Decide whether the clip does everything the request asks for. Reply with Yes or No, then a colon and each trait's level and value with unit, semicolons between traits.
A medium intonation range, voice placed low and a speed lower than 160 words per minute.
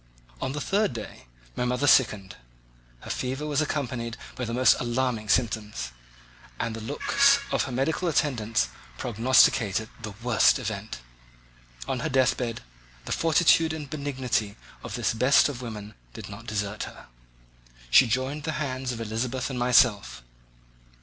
Yes: average, 4.0 semitones; low, 125 Hz; average, 145 wpm